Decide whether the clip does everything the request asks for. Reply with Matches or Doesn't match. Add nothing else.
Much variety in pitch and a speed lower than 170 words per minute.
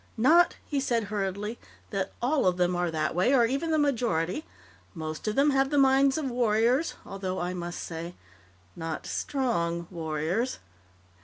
Matches